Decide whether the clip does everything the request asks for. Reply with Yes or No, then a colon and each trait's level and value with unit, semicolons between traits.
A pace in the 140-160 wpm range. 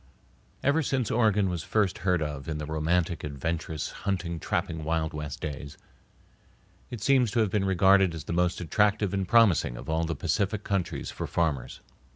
No: average, 175 wpm